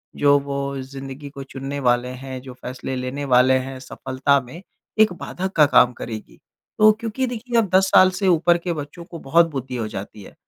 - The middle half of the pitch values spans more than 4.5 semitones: Yes, average, 4.9 semitones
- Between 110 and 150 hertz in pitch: Yes, medium, 140 Hz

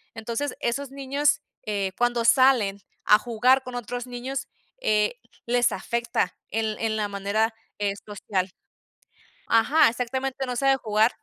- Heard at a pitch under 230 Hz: No, high, 235 Hz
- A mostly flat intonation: No, average, 3.2 semitones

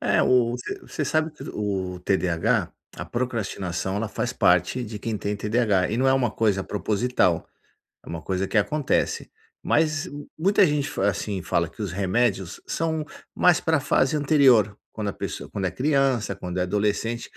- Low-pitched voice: Yes, low, 110 Hz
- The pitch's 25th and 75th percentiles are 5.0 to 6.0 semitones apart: Yes, wide, 5.5 semitones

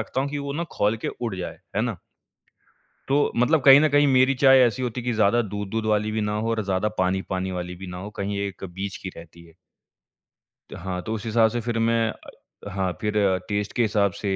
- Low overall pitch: Yes, low, 105 Hz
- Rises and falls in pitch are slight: No, average, 3.7 semitones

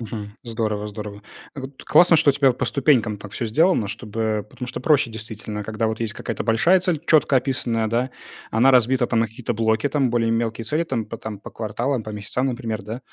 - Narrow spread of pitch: No, average, 3.3 semitones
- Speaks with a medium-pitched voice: No, low, 115 Hz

